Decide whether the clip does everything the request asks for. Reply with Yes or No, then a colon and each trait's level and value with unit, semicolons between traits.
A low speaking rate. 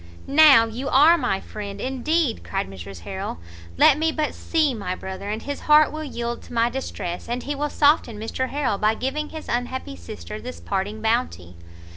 No: average, 185 wpm